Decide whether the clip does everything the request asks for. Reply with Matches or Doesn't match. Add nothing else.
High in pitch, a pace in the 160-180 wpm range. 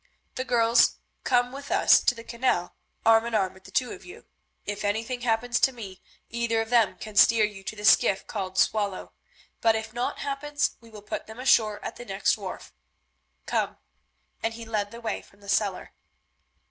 Doesn't match